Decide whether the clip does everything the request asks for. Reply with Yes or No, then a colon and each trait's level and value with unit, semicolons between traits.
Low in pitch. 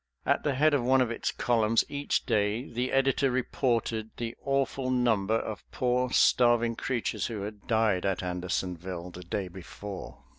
Yes: low, 115 Hz